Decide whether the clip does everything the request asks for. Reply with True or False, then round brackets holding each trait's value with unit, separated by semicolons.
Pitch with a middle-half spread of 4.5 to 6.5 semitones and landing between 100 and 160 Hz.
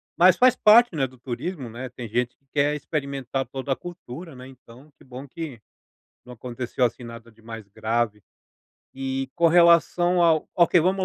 True (5.6 semitones; 135 Hz)